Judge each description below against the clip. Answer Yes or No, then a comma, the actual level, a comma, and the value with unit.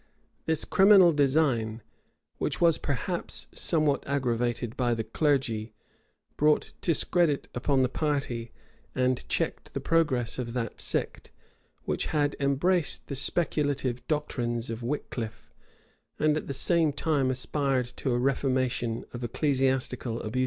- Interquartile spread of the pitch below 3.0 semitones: No, average, 3.8 semitones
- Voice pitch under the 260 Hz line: Yes, low, 135 Hz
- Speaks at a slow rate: Yes, slow, 130 wpm